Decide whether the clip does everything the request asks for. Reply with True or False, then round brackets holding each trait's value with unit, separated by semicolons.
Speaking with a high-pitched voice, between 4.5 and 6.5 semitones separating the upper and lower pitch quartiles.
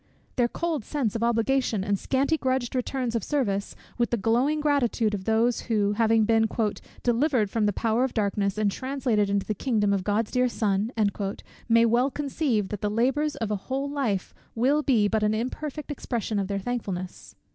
False (230 Hz; 3.9 semitones)